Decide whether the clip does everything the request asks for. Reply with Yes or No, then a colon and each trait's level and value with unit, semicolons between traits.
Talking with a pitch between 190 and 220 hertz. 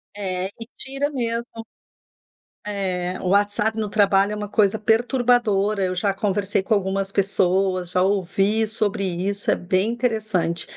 Yes: high, 200 Hz